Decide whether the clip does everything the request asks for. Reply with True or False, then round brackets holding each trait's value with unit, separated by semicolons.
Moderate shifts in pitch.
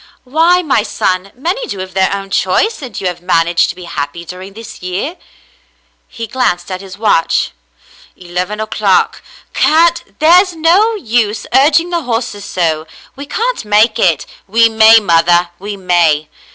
False (7.2 semitones)